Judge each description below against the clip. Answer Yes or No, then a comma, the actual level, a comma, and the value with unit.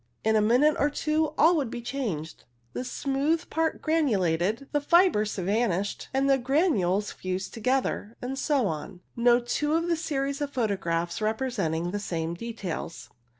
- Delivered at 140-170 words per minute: Yes, average, 160 wpm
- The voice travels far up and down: Yes, wide, 6.9 semitones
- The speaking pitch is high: Yes, high, 240 Hz